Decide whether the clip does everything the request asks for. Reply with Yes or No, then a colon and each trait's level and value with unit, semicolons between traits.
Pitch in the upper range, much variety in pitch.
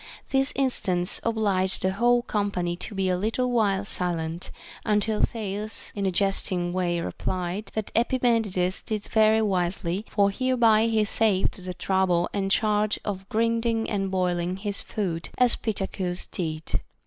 No: high, 200 Hz; average, 3.3 semitones